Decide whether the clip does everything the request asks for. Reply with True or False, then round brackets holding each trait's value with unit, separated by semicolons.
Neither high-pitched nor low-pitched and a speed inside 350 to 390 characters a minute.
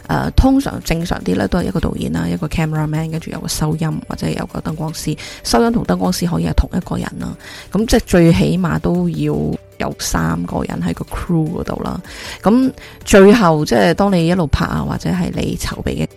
True (155 Hz; 355 characters per minute)